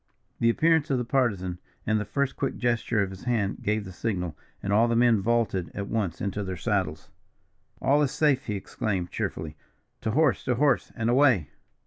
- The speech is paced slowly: No, average, 190 wpm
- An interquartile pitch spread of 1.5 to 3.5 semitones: No, average, 4.4 semitones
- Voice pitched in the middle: No, low, 110 Hz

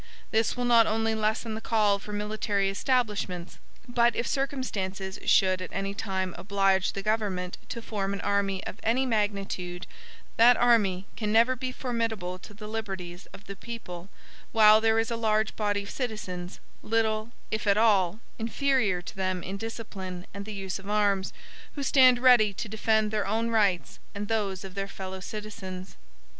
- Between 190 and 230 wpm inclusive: No, average, 170 wpm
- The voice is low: No, high, 210 Hz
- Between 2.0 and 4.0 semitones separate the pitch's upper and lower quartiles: Yes, average, 2.7 semitones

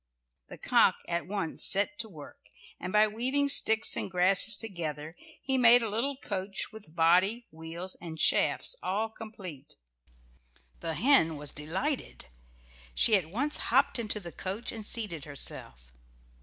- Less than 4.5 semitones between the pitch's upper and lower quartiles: No, wide, 5.6 semitones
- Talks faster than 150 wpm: No, average, 145 wpm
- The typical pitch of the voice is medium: No, high, 195 Hz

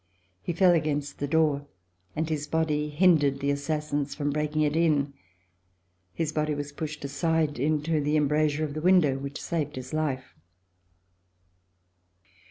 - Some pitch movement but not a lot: No, narrow, 1.6 semitones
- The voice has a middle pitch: Yes, medium, 150 Hz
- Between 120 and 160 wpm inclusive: Yes, average, 155 wpm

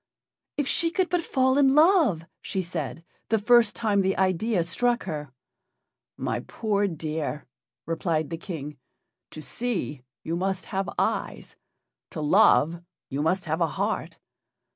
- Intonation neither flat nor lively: No, wide, 6.7 semitones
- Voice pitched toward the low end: No, medium, 185 Hz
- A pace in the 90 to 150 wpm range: Yes, average, 140 wpm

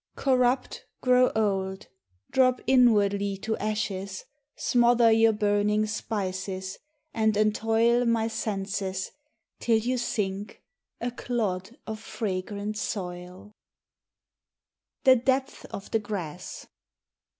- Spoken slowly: Yes, slow, 100 wpm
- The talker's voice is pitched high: Yes, high, 215 Hz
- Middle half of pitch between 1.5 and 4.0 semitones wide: Yes, average, 3.2 semitones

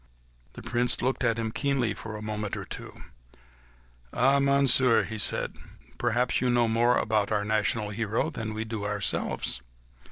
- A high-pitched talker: No, low, 115 Hz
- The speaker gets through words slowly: No, average, 165 wpm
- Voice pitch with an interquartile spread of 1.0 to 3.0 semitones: Yes, narrow, 2.5 semitones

